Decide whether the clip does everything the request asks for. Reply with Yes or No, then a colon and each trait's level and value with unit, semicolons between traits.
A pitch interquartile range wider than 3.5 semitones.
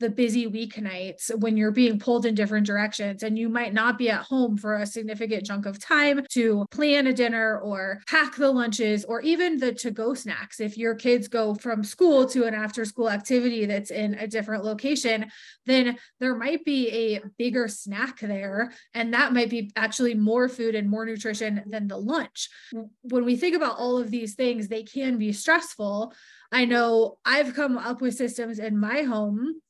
No: narrow, 2.5 semitones